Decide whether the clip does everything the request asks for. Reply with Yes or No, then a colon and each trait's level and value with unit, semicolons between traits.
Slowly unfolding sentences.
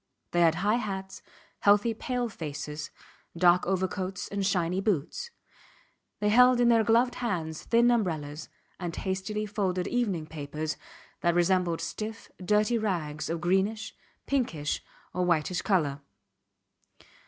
Yes: slow, 125 wpm